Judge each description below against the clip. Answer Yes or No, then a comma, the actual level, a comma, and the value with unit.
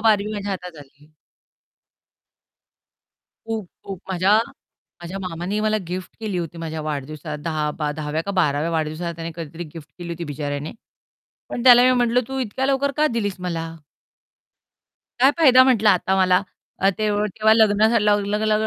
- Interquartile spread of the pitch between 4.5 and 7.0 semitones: Yes, average, 4.9 semitones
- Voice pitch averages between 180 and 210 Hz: Yes, medium, 185 Hz